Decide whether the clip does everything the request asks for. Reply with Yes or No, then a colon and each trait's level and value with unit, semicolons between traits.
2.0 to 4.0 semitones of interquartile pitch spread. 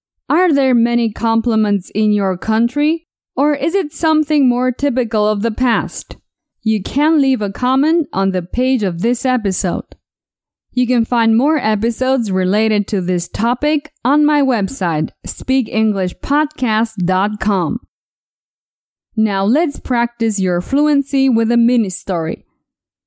No: average, 4.9 semitones